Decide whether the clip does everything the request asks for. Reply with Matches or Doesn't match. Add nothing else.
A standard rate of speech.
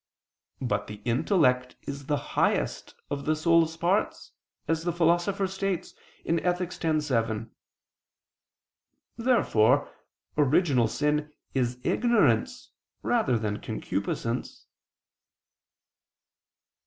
Doesn't match